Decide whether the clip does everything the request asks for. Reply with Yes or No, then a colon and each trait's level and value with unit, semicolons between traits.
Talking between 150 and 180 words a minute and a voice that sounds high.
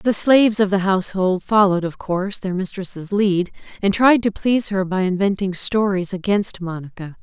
Yes: average, 175 wpm; high, 195 Hz